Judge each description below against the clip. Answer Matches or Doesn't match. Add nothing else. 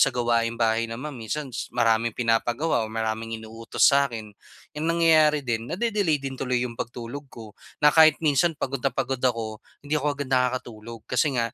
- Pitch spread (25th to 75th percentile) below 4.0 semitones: Doesn't match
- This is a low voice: Matches